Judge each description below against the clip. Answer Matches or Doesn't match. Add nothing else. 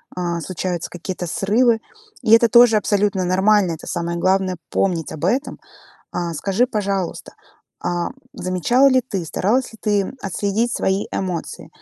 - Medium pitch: Doesn't match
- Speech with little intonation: Doesn't match